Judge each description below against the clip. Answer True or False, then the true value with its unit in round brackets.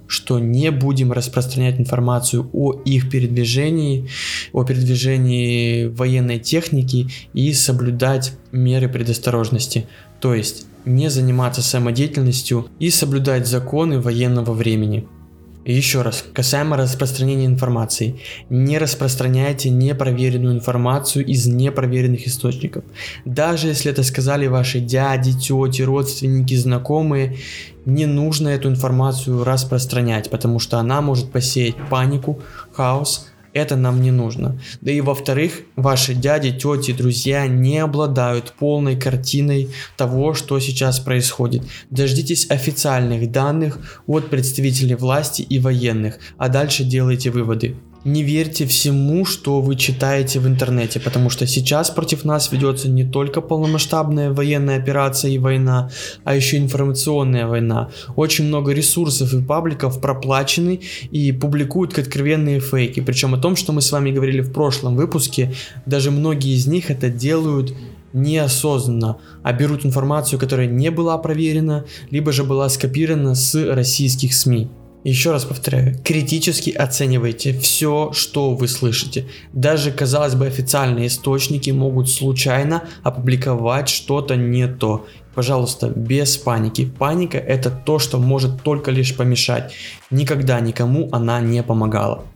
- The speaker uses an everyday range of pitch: False (2.2 semitones)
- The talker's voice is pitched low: True (130 Hz)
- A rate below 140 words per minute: True (125 wpm)